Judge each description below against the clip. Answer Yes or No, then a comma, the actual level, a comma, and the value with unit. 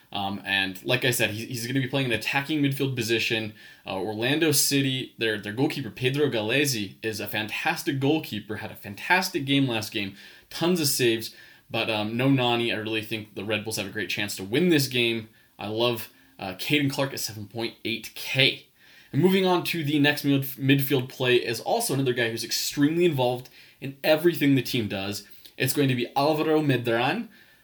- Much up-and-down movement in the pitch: No, average, 4.6 semitones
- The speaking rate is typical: Yes, average, 190 wpm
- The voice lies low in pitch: Yes, low, 125 Hz